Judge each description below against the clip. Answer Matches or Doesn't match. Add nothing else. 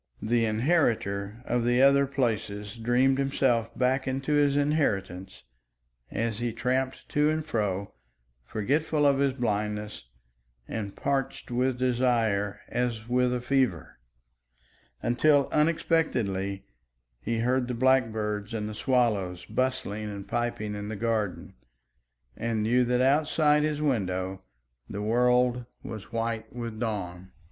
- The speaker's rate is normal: Doesn't match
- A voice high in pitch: Doesn't match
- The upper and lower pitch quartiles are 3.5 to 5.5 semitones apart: Matches